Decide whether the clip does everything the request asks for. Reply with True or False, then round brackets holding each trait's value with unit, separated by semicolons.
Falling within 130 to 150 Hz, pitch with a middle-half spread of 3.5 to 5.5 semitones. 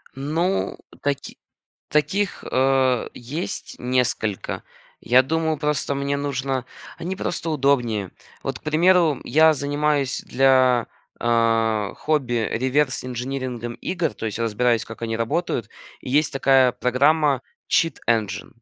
True (135 Hz; 3.9 semitones)